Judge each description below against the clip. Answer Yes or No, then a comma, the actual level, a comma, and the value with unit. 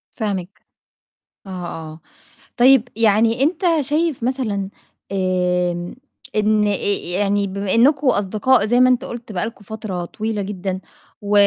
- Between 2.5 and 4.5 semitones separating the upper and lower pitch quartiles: Yes, average, 4.1 semitones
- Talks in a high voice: Yes, high, 210 Hz